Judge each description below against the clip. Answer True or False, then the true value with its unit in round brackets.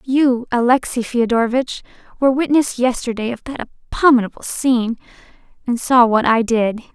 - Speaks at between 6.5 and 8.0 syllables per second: False (5.4 syllables/s)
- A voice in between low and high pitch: False (245 Hz)